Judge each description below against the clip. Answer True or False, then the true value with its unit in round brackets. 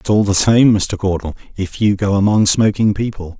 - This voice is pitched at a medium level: False (100 Hz)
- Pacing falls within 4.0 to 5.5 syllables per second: True (5.1 syllables/s)